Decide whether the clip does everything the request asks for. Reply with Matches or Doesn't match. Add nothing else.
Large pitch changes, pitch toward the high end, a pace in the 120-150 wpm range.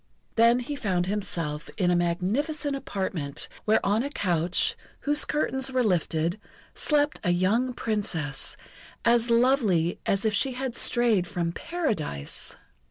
Matches